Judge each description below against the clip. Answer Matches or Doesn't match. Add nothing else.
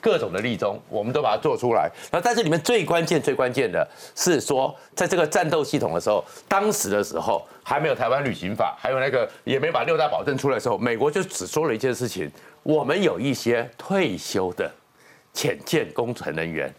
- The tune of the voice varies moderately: Doesn't match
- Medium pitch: Matches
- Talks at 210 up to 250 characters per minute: Doesn't match